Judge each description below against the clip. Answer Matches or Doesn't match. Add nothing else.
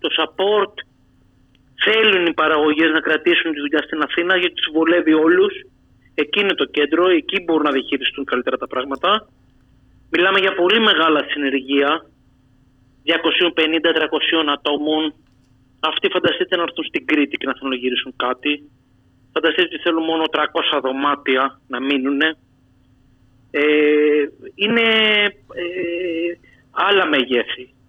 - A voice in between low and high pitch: Matches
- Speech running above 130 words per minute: Doesn't match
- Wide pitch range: Doesn't match